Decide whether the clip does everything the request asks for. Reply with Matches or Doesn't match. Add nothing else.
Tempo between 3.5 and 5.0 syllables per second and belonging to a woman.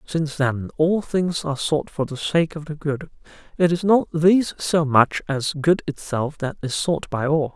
Doesn't match